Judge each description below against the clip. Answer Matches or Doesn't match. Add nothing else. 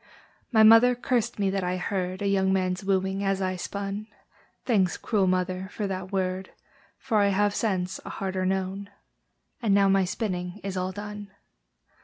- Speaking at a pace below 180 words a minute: Matches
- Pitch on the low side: Doesn't match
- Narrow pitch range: Matches